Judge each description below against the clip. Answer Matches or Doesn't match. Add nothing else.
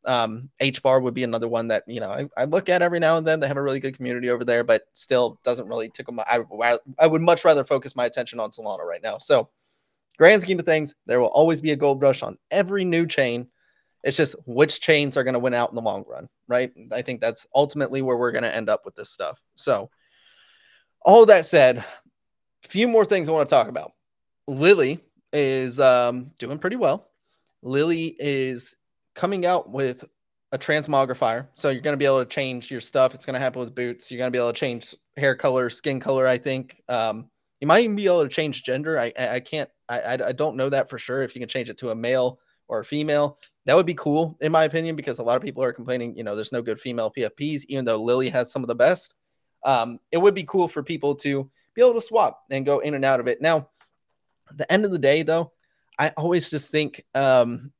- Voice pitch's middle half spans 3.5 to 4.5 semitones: Matches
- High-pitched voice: Doesn't match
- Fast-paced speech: Matches